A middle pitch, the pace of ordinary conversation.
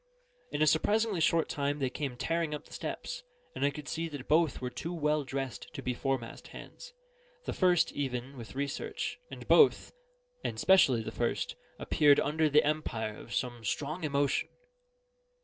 Yes: medium, 145 Hz; average, 170 wpm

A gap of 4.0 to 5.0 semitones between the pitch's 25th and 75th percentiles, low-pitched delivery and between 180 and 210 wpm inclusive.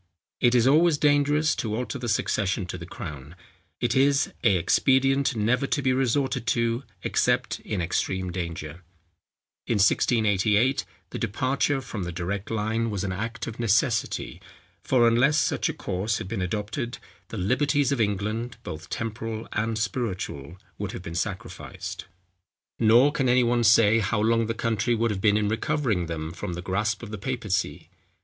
No: average, 4.3 semitones; low, 110 Hz; average, 165 wpm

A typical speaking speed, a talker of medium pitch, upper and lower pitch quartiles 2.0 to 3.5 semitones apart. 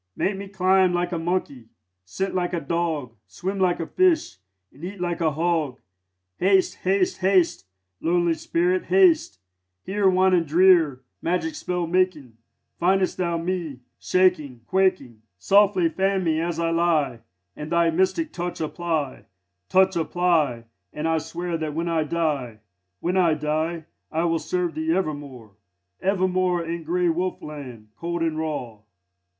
Yes: average, 150 wpm; medium, 170 Hz; average, 2.9 semitones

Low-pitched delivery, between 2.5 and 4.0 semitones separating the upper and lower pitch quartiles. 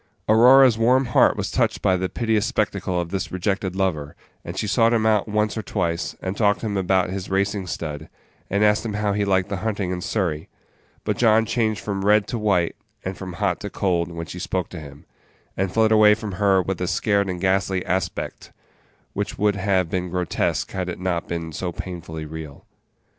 Yes: very low, 95 Hz; average, 2.8 semitones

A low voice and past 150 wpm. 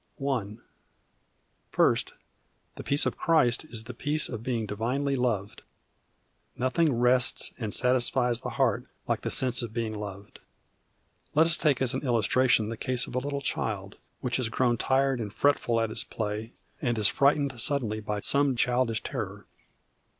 Yes: low, 125 Hz; average, 160 wpm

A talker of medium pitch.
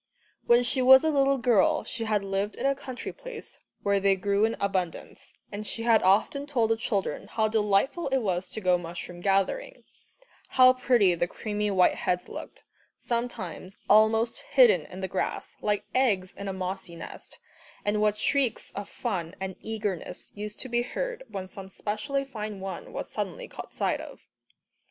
No: high, 210 Hz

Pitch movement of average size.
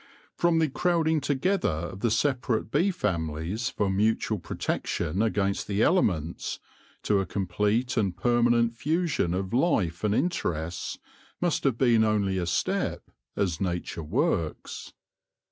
No: wide, 6.3 semitones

